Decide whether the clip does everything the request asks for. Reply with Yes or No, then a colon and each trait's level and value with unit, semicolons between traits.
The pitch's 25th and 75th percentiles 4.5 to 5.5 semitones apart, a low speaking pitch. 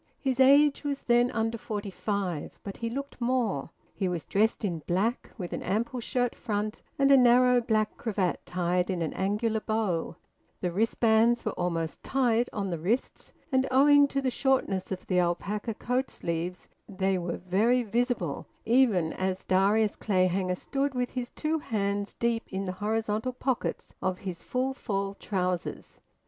No: average, 4.9 semitones; high, 215 Hz